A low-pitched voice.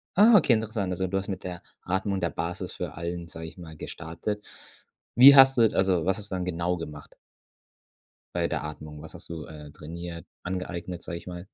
Yes: very low, 90 Hz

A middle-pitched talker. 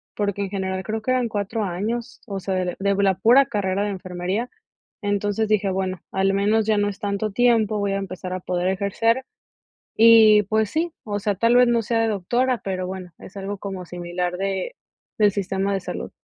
No: high, 200 Hz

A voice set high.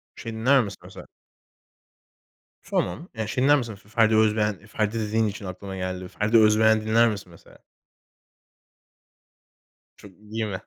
No: low, 110 Hz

